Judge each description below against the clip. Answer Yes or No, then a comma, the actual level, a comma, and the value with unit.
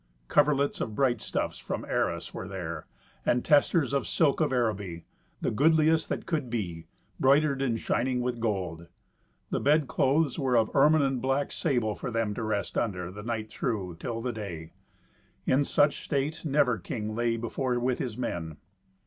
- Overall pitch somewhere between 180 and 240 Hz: No, low, 120 Hz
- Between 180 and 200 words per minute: No, average, 170 wpm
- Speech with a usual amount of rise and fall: Yes, average, 4.7 semitones